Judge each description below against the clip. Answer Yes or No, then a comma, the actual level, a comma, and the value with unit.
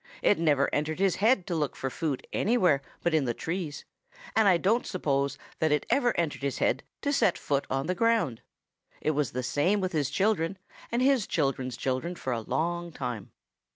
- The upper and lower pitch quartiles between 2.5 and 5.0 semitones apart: No, wide, 5.6 semitones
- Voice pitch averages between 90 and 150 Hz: No, medium, 160 Hz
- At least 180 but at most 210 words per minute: Yes, average, 195 wpm